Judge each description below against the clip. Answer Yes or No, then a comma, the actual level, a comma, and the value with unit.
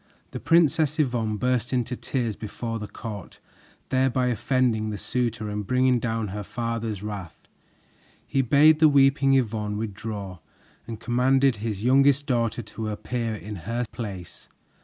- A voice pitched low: Yes, low, 115 Hz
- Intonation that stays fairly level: No, average, 3.3 semitones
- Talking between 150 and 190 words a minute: No, average, 140 wpm